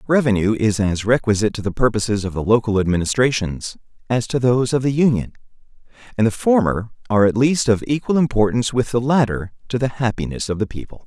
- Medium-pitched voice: No, low, 115 Hz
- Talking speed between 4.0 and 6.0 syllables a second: No, 6.3 syllables/s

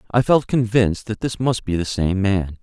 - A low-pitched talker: Yes, low, 105 Hz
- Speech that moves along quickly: Yes, fast, 230 wpm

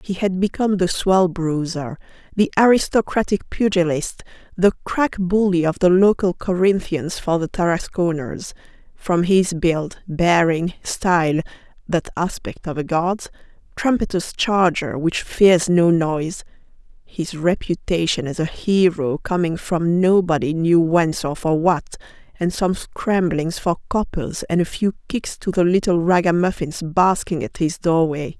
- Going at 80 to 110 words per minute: No, slow, 135 wpm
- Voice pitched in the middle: Yes, medium, 175 Hz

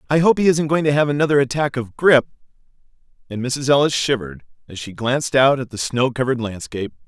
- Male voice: Yes, male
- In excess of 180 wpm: Yes, fast, 205 wpm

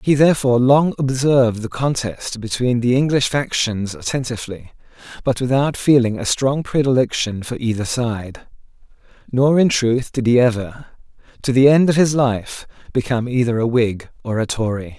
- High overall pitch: No, low, 125 Hz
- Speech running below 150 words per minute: No, average, 155 wpm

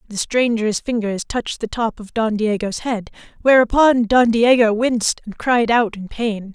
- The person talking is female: Yes, female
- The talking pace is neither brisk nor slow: Yes, average, 175 wpm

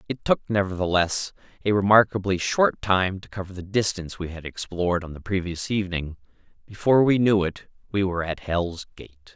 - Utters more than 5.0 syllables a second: Yes, 5.5 syllables/s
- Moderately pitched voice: No, very low, 95 Hz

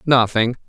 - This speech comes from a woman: No, male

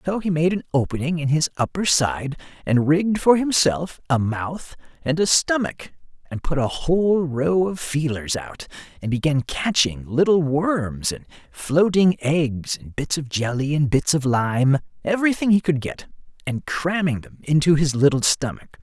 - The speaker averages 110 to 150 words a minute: No, average, 165 wpm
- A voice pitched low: No, medium, 150 Hz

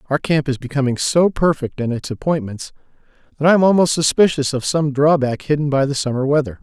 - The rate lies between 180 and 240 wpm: Yes, average, 200 wpm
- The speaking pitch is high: No, medium, 145 Hz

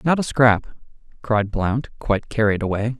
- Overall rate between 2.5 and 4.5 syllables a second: No, 4.9 syllables/s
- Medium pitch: No, low, 115 Hz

